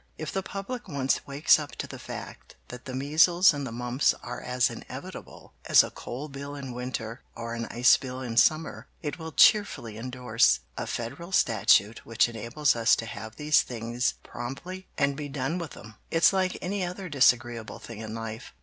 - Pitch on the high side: No, low, 130 Hz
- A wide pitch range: No, average, 4.7 semitones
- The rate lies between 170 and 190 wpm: Yes, average, 185 wpm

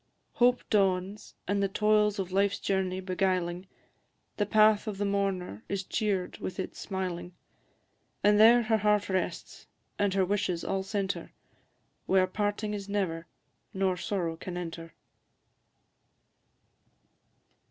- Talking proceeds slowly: Yes, slow, 125 wpm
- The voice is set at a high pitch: Yes, high, 195 Hz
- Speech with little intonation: Yes, narrow, 2.0 semitones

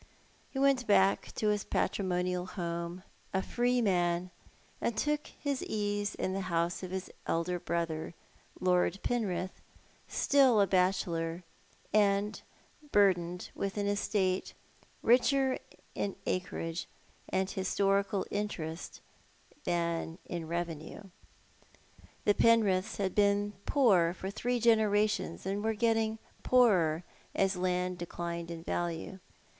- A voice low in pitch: No, high, 190 Hz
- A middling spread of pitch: Yes, average, 3.3 semitones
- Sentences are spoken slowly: Yes, slow, 115 wpm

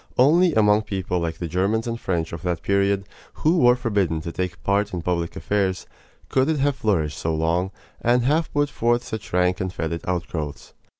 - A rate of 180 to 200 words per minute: Yes, average, 190 wpm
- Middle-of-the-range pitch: No, low, 100 Hz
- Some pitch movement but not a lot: No, wide, 5.8 semitones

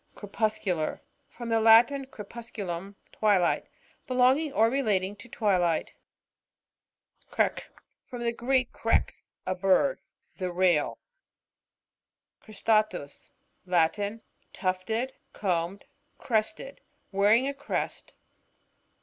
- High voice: Yes, high, 215 Hz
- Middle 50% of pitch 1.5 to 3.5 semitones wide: No, average, 4.2 semitones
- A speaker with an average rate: No, slow, 90 wpm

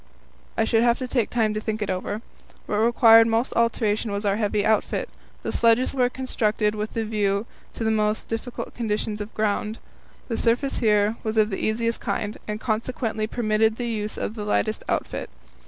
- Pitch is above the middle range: Yes, high, 220 Hz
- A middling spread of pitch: No, narrow, 1.5 semitones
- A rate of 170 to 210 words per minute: Yes, average, 190 wpm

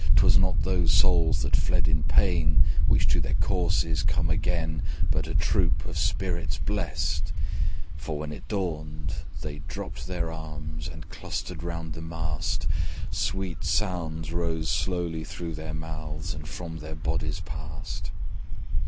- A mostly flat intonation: Yes, narrow, 1.9 semitones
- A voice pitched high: No, very low, 80 Hz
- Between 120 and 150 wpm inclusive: Yes, average, 145 wpm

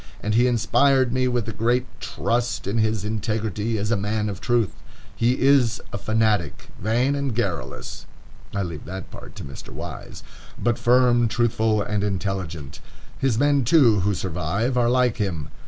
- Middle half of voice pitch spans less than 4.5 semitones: Yes, average, 3.3 semitones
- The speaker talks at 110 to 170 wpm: Yes, average, 160 wpm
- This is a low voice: Yes, low, 110 Hz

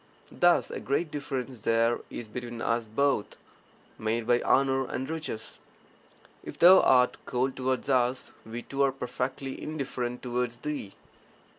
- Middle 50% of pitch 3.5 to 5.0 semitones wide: No, narrow, 2.4 semitones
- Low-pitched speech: Yes, low, 125 Hz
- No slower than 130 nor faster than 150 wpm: Yes, average, 140 wpm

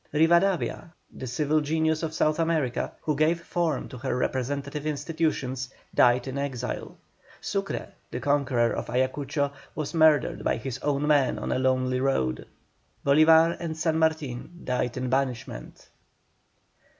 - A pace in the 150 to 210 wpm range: No, average, 140 wpm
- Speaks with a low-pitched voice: No, medium, 145 Hz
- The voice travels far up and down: No, average, 3.6 semitones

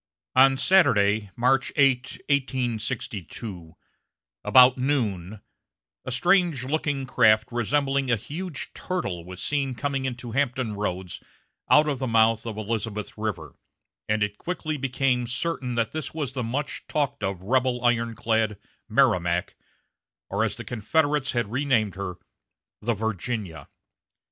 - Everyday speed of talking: No, slow, 130 wpm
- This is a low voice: Yes, low, 120 Hz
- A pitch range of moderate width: Yes, average, 4.2 semitones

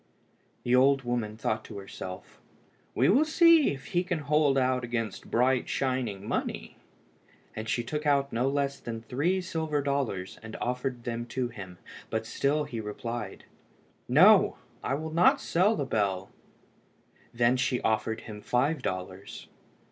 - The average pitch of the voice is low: Yes, low, 125 Hz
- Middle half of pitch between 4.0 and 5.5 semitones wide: Yes, average, 4.3 semitones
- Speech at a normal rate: Yes, average, 150 wpm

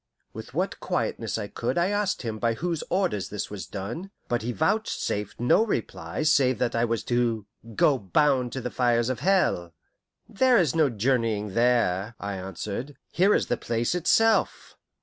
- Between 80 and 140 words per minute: No, average, 170 wpm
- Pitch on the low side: Yes, low, 120 Hz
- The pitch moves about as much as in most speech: No, wide, 7.0 semitones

